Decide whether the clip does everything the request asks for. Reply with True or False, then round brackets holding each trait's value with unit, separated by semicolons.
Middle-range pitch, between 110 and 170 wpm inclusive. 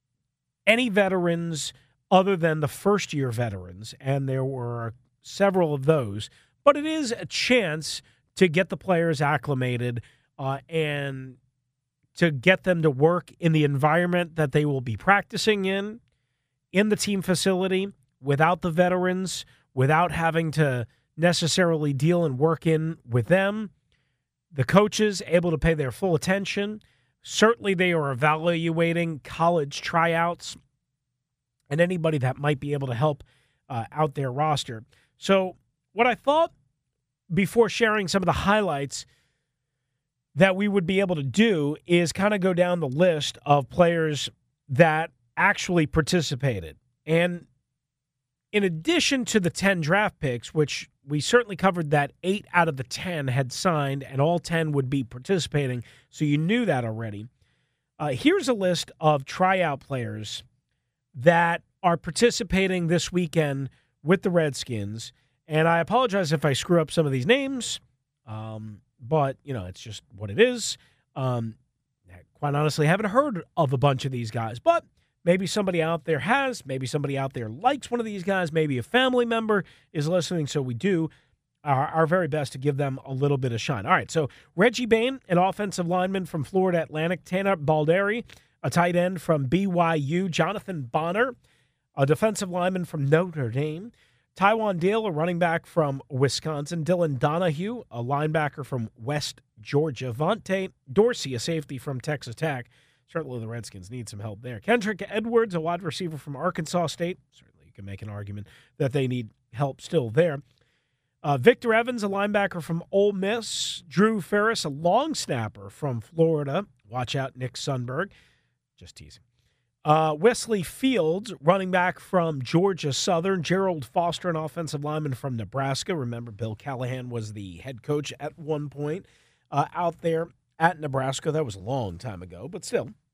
True (155 Hz; 160 wpm)